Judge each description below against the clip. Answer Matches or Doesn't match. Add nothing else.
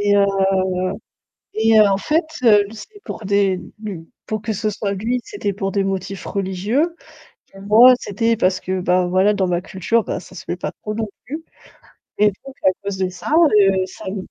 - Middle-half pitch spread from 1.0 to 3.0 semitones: Matches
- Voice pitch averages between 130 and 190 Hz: Doesn't match